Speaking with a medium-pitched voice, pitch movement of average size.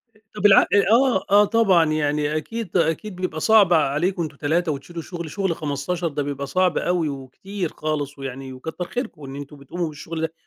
Yes: medium, 160 Hz; average, 4.1 semitones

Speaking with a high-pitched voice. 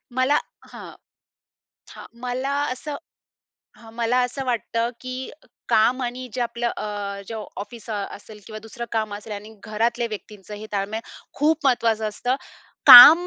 Yes: high, 235 Hz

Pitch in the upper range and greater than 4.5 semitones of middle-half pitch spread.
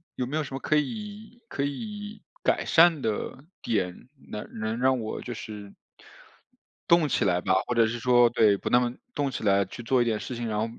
No: low, 120 Hz; average, 5.2 semitones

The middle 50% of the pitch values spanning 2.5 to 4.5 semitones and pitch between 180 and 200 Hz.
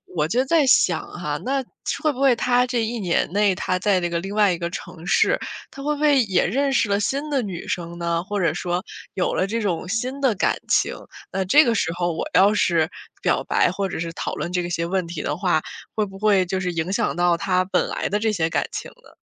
No: average, 4.9 semitones; high, 190 Hz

